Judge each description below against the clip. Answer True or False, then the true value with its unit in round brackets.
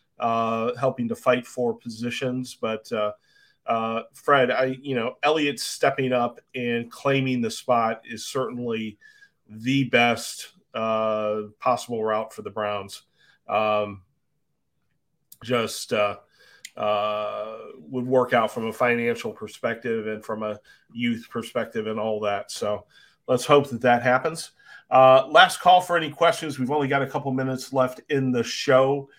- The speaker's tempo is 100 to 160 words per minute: True (145 wpm)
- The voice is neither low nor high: False (125 Hz)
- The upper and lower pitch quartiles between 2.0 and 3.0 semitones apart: False (3.7 semitones)